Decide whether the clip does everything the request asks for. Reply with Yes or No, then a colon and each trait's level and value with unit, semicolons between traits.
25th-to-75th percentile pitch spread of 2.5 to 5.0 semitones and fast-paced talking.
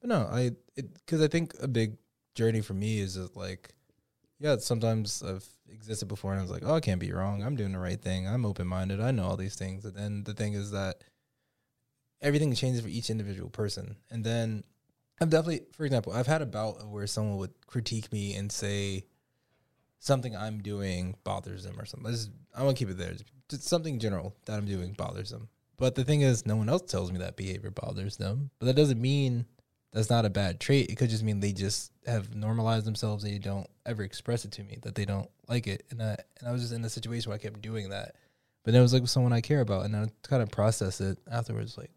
Yes: average, 3.8 semitones; fast, 240 wpm